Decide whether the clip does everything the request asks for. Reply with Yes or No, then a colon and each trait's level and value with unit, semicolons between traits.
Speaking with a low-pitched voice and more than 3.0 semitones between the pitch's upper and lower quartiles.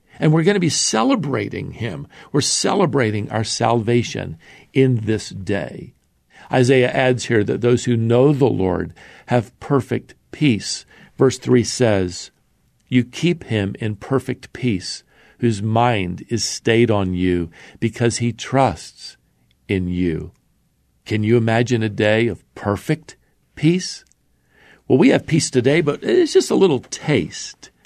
Yes: low, 120 Hz; average, 4.1 semitones